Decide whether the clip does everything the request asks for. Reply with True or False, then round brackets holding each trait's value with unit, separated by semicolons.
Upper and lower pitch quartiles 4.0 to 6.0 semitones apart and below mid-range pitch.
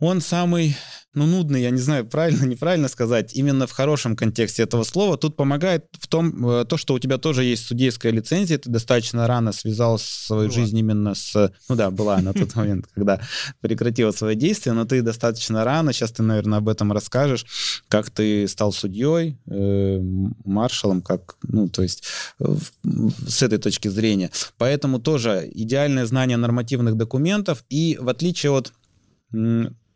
True (4.6 semitones; 120 Hz)